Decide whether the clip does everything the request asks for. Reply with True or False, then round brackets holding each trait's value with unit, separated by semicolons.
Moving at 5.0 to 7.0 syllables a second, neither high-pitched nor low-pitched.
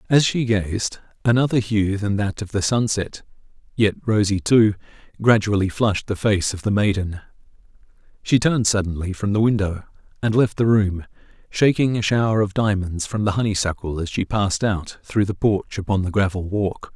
False (5.1 syllables/s; 105 Hz)